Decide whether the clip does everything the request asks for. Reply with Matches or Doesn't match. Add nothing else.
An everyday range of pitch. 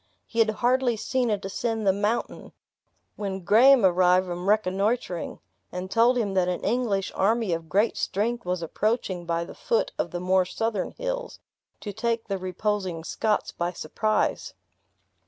Matches